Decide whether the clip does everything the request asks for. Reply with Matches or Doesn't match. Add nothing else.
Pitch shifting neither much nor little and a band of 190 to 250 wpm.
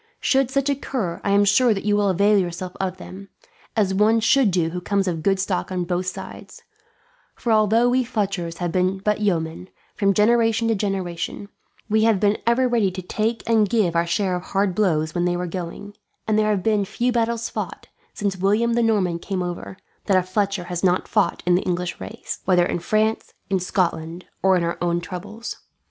Matches